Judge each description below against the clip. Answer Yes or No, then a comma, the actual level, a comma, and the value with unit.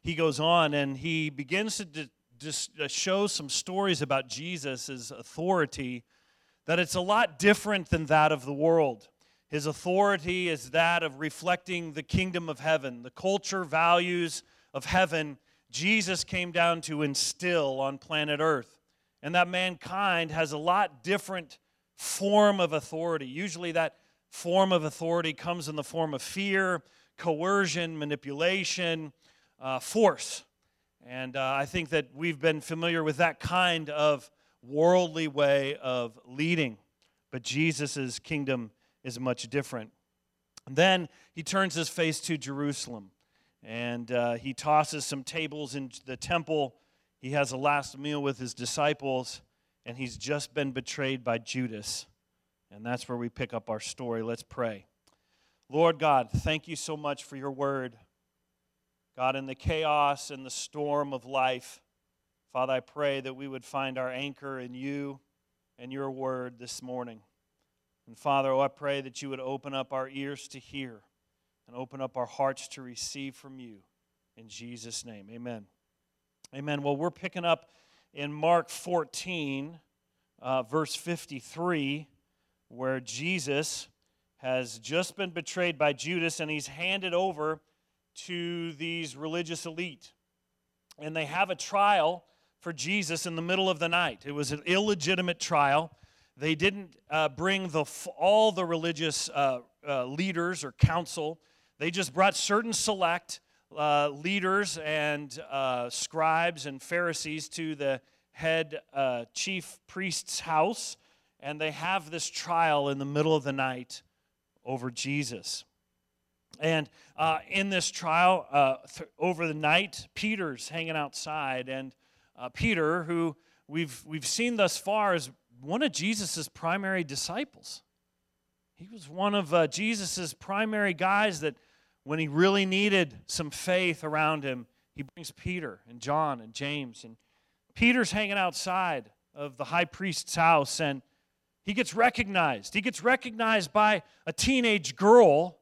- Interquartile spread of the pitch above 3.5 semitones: Yes, average, 4.7 semitones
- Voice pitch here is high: No, medium, 155 Hz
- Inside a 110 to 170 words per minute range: Yes, average, 150 wpm